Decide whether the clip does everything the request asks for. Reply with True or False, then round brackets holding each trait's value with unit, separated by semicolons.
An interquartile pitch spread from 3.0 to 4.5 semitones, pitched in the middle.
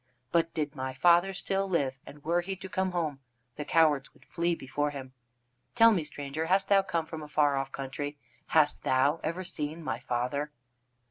True (3.6 semitones; 155 Hz)